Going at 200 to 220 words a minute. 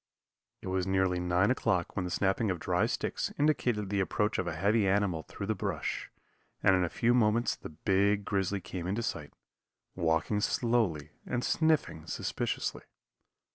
No: average, 165 wpm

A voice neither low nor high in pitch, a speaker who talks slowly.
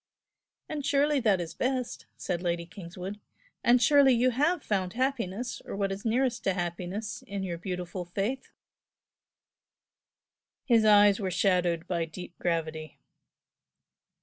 No: high, 195 Hz; slow, 130 wpm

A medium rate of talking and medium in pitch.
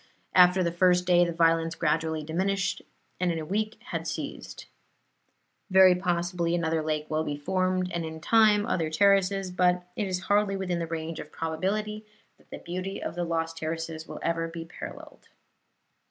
Yes: average, 170 wpm; medium, 175 Hz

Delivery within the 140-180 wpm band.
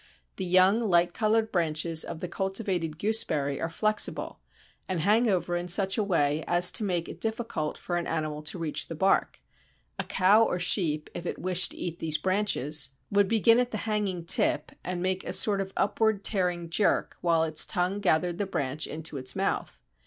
No: average, 190 wpm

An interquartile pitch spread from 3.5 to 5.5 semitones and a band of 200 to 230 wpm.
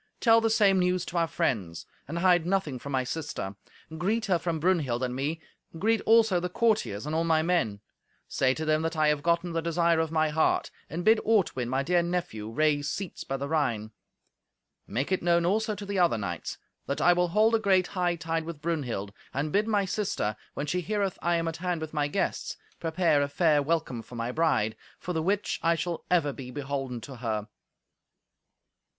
Yes: average, 4.2 semitones; fast, 205 wpm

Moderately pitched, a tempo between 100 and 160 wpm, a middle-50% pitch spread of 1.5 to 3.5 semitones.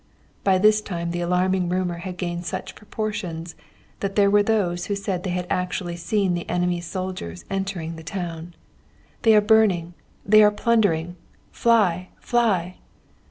Yes: medium, 180 Hz; average, 155 wpm; average, 2.9 semitones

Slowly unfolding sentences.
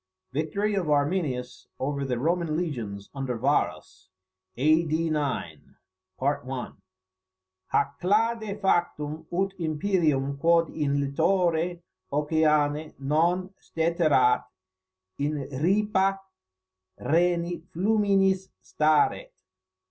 Yes: slow, 80 wpm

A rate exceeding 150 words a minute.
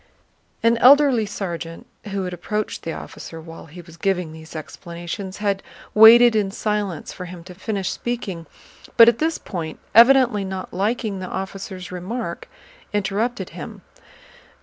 No: average, 145 wpm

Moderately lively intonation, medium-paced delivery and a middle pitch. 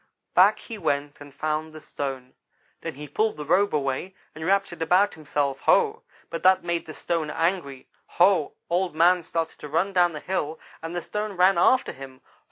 Yes: average, 3.8 semitones; average, 190 wpm; medium, 165 Hz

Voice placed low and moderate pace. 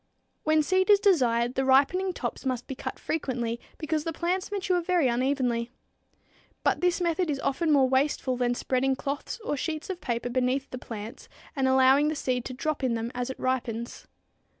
No: very high, 270 Hz; average, 185 wpm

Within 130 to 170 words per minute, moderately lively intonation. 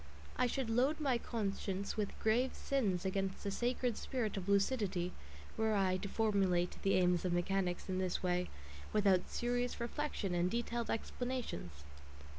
Yes: average, 150 wpm; average, 4.4 semitones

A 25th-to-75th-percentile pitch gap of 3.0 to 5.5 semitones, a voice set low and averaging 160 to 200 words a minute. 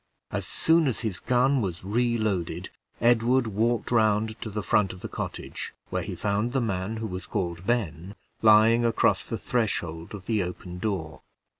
Yes: average, 4.0 semitones; low, 110 Hz; average, 170 wpm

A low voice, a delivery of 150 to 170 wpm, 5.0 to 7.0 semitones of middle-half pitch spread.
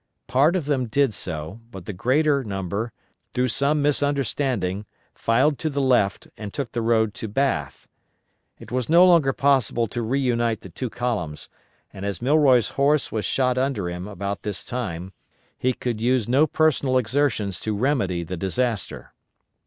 Yes: low, 120 Hz; average, 160 wpm; wide, 5.4 semitones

